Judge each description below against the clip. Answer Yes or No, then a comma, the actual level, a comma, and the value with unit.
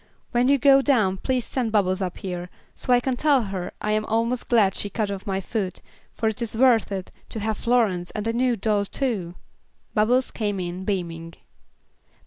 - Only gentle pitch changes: No, average, 4.2 semitones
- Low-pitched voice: No, high, 215 Hz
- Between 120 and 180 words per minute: No, average, 190 wpm